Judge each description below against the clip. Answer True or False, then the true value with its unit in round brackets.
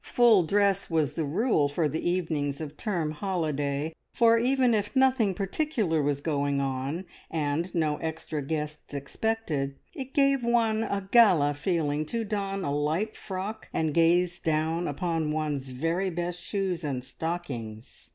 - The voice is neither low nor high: True (165 Hz)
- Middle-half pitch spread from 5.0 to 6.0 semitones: True (5.5 semitones)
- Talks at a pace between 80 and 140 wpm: False (150 wpm)